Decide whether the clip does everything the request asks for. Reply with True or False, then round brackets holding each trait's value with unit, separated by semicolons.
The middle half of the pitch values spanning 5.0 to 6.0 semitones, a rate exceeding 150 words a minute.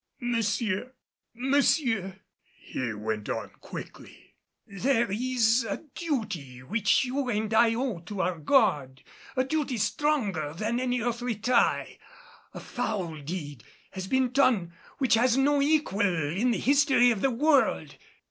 False (5.6 semitones; 135 wpm)